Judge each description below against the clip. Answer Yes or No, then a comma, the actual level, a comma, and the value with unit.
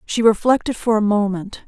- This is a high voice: Yes, high, 215 Hz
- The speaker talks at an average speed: Yes, average, 180 wpm